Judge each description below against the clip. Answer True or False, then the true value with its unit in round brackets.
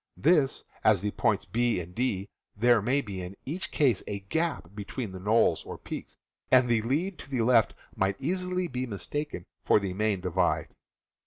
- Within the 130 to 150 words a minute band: False (175 wpm)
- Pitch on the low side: True (115 Hz)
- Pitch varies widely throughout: True (5.8 semitones)